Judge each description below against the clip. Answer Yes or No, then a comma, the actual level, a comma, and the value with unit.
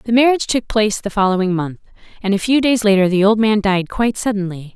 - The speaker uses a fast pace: Yes, fast, 225 wpm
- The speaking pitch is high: Yes, high, 210 Hz